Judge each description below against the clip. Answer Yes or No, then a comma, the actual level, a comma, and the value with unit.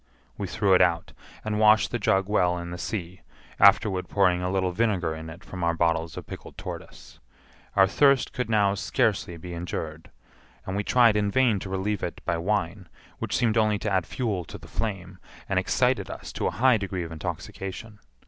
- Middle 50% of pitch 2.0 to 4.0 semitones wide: Yes, average, 3.3 semitones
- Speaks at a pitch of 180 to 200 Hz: No, very low, 95 Hz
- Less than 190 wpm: No, average, 195 wpm